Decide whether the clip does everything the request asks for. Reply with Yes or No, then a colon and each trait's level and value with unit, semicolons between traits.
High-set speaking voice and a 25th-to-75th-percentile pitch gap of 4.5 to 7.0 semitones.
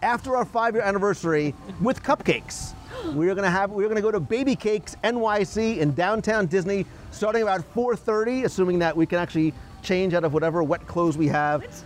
Yes: high, 195 Hz; average, 4.8 semitones